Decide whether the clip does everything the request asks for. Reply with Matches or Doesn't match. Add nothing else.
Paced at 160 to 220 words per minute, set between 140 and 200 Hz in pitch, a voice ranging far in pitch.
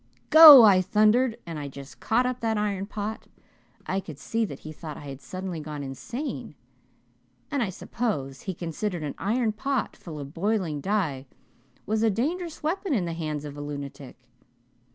Matches